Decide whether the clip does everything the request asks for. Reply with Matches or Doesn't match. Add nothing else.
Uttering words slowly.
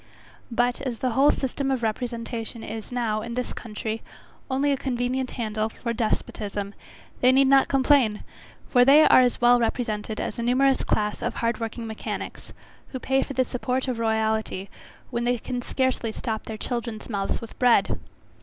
Doesn't match